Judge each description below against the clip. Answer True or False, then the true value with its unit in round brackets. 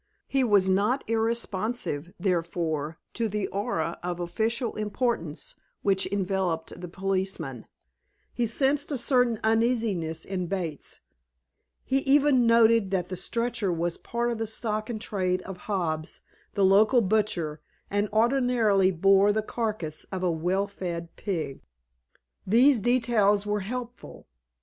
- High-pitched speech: True (200 Hz)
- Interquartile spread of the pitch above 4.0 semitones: True (4.5 semitones)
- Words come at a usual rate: False (130 wpm)